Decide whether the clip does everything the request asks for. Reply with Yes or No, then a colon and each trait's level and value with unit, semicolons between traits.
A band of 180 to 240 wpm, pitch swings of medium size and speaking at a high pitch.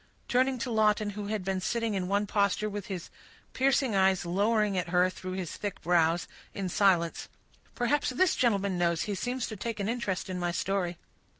Yes: average, 185 wpm; average, 3.4 semitones; high, 200 Hz